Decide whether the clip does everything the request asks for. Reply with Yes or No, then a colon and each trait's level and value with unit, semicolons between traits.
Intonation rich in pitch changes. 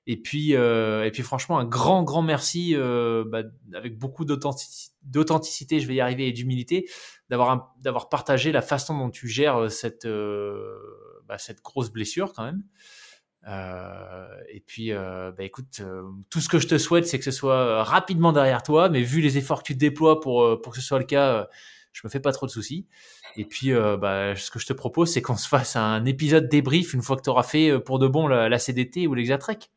No: average, 4.8 semitones